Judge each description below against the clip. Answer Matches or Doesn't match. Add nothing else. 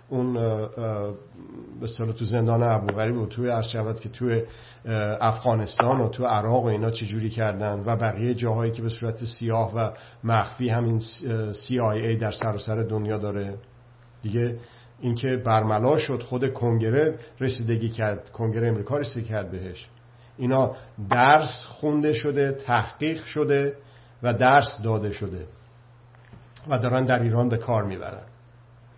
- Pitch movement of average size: Doesn't match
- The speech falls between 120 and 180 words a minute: Matches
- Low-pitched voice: Matches